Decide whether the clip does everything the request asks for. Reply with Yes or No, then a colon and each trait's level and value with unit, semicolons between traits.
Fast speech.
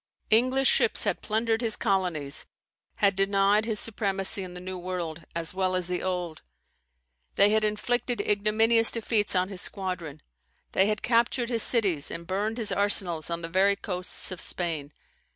No: average, 165 wpm